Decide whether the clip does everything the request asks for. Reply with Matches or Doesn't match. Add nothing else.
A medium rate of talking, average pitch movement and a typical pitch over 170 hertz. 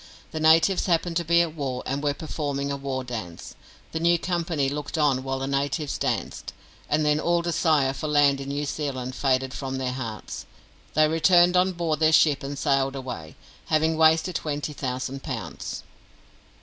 Doesn't match